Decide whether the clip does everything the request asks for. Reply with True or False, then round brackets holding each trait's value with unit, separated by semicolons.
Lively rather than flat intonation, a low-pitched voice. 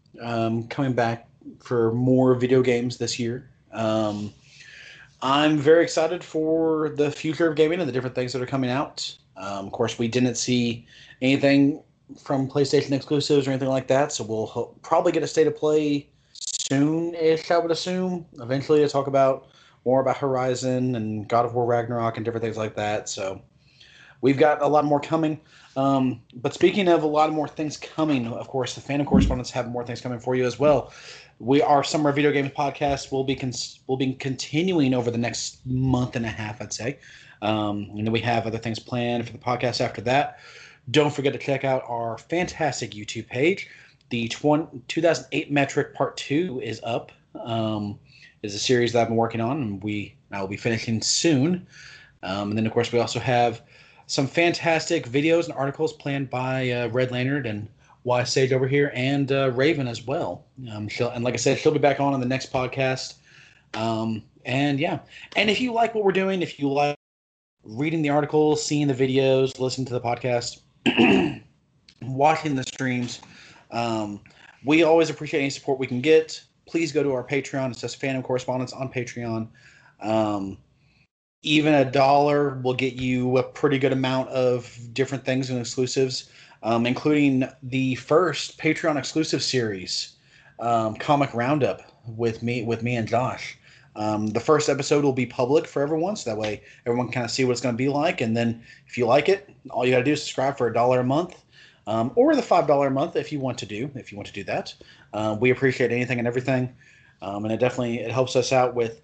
False (3.4 semitones; 130 Hz)